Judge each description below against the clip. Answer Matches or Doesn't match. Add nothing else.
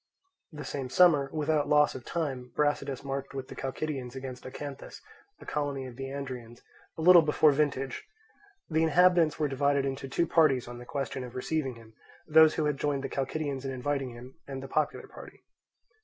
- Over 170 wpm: Matches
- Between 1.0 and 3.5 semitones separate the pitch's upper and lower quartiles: Matches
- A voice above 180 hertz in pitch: Doesn't match